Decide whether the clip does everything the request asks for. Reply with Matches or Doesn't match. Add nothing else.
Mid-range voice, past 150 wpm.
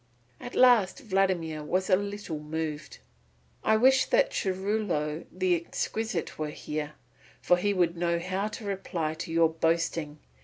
Doesn't match